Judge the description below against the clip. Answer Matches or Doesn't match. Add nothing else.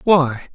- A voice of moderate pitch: Matches